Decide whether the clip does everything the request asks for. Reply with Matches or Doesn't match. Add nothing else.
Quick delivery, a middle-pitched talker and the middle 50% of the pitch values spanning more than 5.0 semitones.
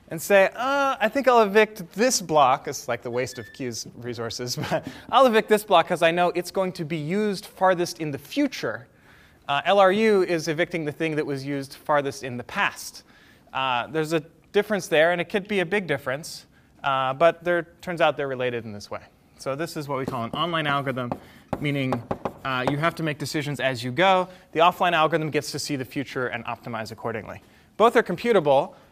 Matches